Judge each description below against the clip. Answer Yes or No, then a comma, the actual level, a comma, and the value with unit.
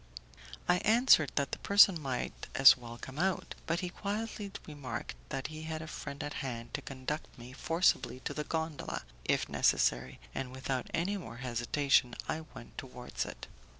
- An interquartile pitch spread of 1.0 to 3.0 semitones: No, average, 4.8 semitones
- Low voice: No, medium, 145 Hz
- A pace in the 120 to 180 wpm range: Yes, average, 170 wpm